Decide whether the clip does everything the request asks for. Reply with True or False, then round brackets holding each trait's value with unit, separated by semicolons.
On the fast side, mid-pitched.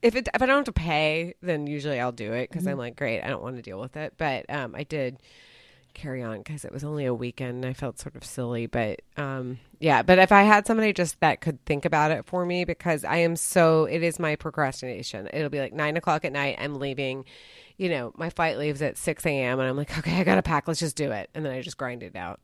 True (275 wpm; 150 Hz)